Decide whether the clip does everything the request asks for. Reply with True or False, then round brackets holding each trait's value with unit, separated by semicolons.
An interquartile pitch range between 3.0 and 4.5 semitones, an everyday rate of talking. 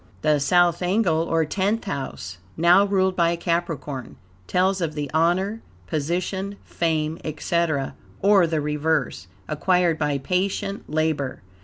False (3.4 semitones; 125 wpm)